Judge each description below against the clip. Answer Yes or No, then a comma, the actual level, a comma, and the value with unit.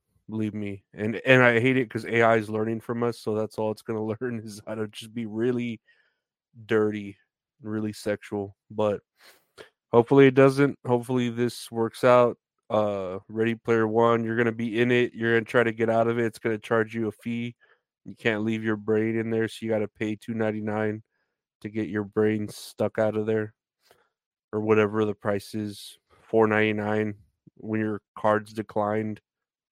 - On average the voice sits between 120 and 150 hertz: No, low, 110 Hz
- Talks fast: No, average, 190 wpm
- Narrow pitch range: Yes, narrow, 1.4 semitones